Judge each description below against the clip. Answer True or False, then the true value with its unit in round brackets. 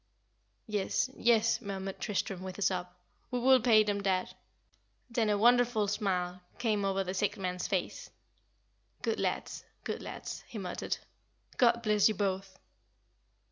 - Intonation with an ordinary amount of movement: True (3.0 semitones)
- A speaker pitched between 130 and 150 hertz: False (205 Hz)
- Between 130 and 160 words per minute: True (140 wpm)